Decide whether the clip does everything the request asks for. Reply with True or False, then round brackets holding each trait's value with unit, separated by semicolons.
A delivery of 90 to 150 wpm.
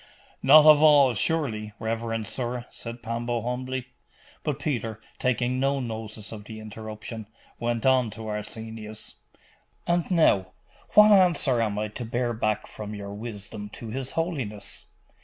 True (140 wpm)